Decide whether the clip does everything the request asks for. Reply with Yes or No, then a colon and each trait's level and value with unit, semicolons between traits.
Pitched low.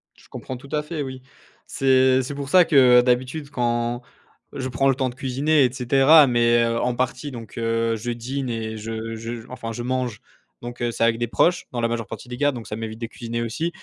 Yes: low, 125 Hz